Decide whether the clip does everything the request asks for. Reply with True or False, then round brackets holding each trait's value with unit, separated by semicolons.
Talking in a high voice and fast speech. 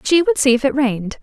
True (270 Hz; 295 wpm)